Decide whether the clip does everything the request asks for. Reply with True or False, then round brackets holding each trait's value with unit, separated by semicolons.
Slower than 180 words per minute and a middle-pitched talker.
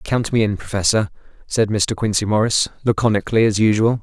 False (165 wpm; 105 Hz)